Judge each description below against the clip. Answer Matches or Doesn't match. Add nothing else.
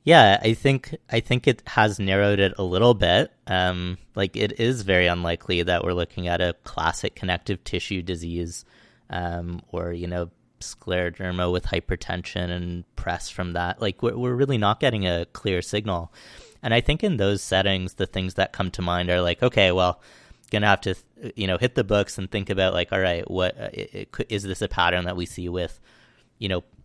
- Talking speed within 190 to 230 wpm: Matches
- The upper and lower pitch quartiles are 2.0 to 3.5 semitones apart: Matches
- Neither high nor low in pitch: Doesn't match